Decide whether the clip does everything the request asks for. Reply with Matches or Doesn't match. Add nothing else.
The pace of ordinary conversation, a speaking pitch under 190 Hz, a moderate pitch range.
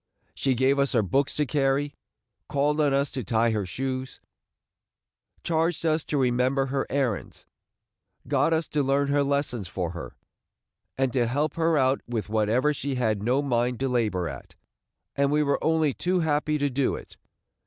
Matches